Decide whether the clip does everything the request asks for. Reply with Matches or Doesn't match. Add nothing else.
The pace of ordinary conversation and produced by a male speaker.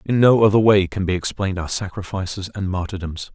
Matches